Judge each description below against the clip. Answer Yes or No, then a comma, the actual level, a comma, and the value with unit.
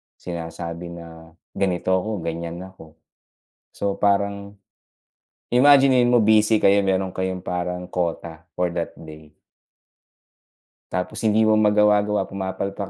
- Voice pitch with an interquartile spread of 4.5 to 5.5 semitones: No, average, 3.4 semitones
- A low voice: Yes, very low, 95 Hz